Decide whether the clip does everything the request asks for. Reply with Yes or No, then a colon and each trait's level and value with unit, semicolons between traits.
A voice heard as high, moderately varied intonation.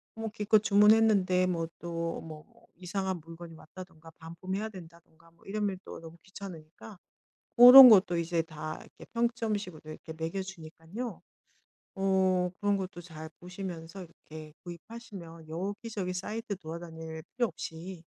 No: medium, 180 Hz; average, 3.7 semitones